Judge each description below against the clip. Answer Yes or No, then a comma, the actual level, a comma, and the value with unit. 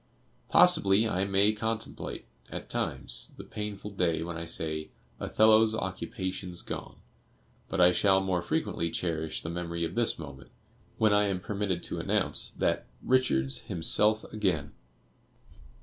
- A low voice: Yes, very low, 95 Hz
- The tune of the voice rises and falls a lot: No, average, 4.0 semitones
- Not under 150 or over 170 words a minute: No, slow, 135 wpm